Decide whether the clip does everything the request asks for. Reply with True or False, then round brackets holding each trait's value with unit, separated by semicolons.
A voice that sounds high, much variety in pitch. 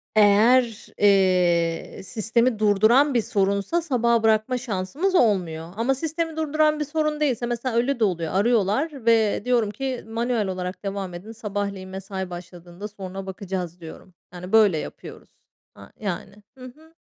False (215 Hz; 4.8 semitones)